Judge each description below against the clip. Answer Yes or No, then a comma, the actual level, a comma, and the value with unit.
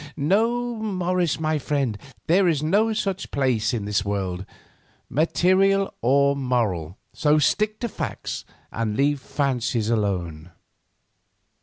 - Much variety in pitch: Yes, wide, 9.0 semitones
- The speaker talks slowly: Yes, slow, 120 wpm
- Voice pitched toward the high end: No, medium, 140 Hz